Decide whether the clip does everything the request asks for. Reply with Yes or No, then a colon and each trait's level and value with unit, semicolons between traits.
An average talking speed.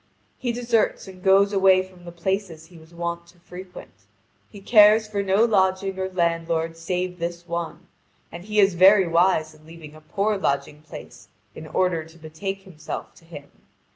Yes: average, 175 wpm